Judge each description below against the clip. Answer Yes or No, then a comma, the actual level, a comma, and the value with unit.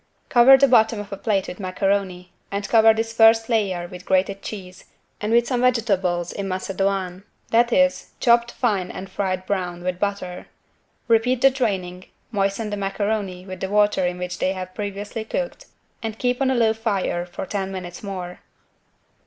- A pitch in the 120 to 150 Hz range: No, high, 200 Hz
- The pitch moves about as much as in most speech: Yes, average, 3.3 semitones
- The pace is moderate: Yes, average, 175 wpm